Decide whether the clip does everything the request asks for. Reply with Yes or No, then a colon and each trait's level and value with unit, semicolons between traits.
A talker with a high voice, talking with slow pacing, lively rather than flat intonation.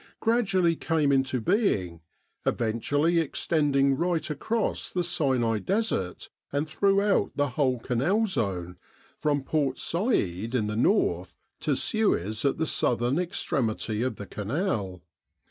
No: medium, 140 Hz; slow, 125 wpm; wide, 7.6 semitones